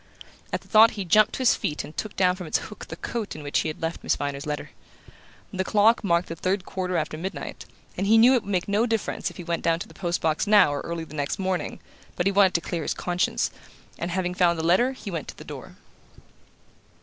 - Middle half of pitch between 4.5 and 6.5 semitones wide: No, average, 3.7 semitones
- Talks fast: Yes, fast, 250 wpm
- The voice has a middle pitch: Yes, medium, 180 Hz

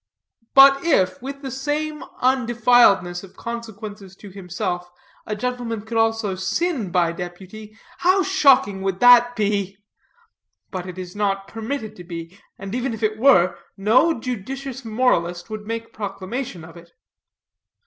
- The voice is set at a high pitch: Yes, high, 215 Hz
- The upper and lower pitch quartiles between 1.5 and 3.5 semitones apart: No, average, 4.9 semitones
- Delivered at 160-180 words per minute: No, average, 140 wpm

